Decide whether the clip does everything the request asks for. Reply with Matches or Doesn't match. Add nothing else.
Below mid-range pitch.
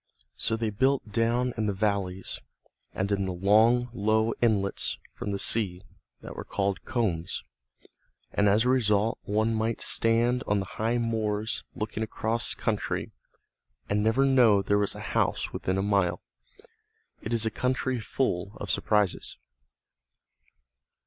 Matches